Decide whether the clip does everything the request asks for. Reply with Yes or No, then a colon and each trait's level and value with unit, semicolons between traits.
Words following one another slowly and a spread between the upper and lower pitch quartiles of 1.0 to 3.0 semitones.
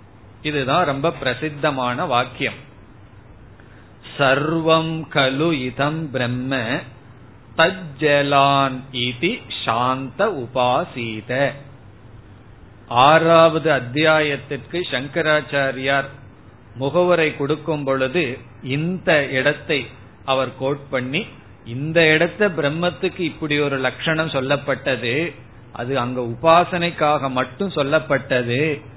No: slow, 60 wpm; average, 4.1 semitones